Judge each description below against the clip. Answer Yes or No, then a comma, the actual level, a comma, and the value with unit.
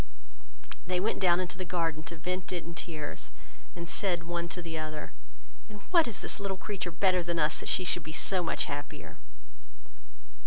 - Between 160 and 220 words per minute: Yes, average, 190 wpm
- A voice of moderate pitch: Yes, medium, 175 Hz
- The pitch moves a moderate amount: No, narrow, 2.0 semitones